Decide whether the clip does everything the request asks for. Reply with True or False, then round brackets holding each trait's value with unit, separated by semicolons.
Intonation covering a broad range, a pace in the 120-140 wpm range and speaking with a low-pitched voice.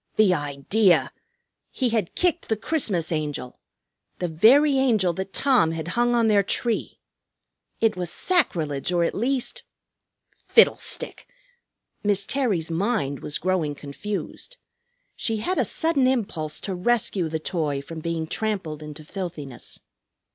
False (6.8 semitones; 135 wpm; 190 Hz)